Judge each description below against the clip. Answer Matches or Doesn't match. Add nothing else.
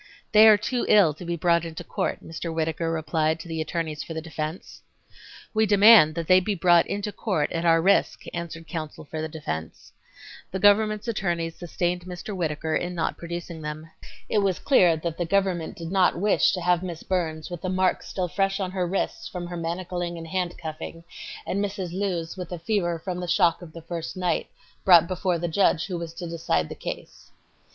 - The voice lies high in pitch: Doesn't match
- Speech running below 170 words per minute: Doesn't match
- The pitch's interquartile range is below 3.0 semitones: Matches